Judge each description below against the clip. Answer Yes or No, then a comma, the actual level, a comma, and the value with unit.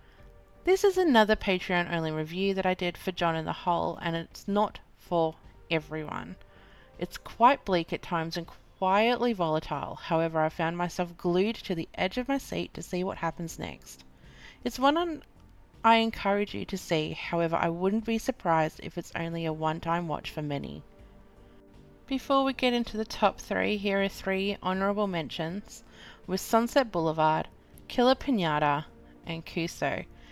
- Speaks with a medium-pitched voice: Yes, medium, 180 Hz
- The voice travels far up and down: No, average, 4.8 semitones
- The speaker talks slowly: No, average, 160 wpm